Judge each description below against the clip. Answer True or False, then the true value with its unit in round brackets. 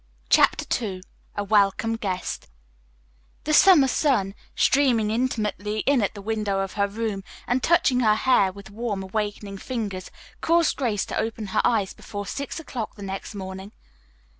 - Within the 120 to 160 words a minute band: True (155 wpm)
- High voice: True (215 Hz)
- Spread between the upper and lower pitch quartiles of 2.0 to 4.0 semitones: True (3.6 semitones)